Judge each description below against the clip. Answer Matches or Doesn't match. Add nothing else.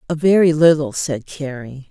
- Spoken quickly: Doesn't match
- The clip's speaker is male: Doesn't match